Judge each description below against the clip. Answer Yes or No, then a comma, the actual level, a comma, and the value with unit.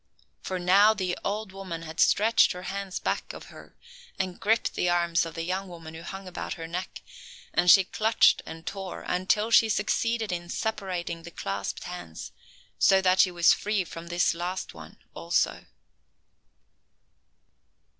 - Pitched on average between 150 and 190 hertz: Yes, medium, 185 Hz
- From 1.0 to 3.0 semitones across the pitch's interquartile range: Yes, narrow, 2.5 semitones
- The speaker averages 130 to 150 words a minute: No, average, 160 wpm